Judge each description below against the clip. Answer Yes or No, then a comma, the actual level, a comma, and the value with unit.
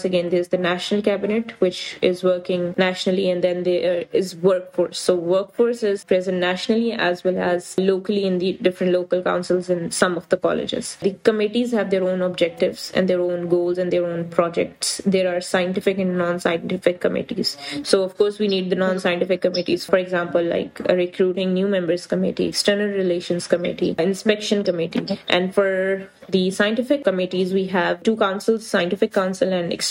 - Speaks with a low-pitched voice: No, medium, 185 Hz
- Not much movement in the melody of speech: Yes, narrow, 1.7 semitones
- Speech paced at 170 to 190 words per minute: Yes, average, 175 wpm